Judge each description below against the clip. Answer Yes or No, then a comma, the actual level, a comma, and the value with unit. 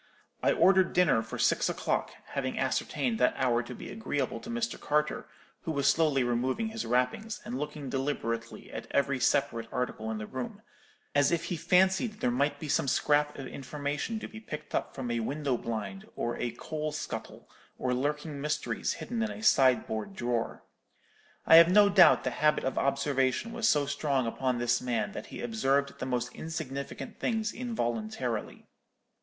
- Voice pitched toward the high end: No, medium, 140 Hz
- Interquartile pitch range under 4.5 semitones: No, average, 4.8 semitones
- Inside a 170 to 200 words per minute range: Yes, average, 175 wpm